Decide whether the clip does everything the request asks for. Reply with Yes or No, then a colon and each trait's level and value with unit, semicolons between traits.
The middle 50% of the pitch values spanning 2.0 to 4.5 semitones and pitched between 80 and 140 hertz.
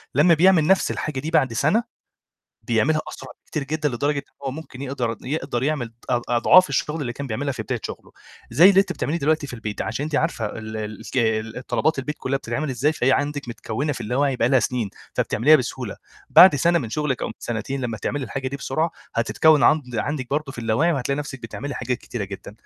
Yes: average, 4.1 semitones; low, 135 Hz